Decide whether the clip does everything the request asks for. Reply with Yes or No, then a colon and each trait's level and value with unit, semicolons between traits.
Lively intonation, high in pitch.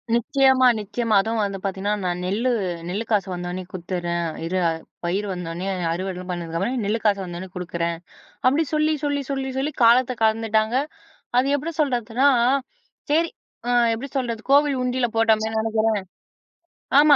Yes: wide, 5.9 semitones; high, 220 Hz